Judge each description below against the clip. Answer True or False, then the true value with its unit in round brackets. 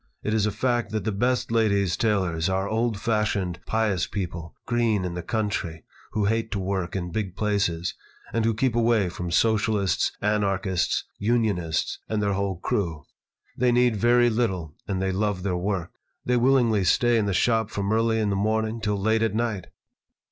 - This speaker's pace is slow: False (180 wpm)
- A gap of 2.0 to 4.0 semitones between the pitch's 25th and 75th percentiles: True (3.0 semitones)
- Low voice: True (105 Hz)